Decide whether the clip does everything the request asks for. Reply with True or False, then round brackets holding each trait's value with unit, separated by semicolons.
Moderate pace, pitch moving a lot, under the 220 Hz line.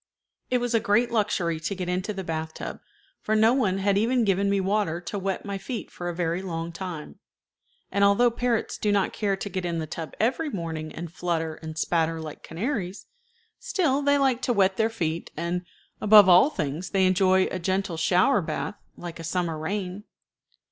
False (195 wpm; 3.9 semitones; 190 Hz)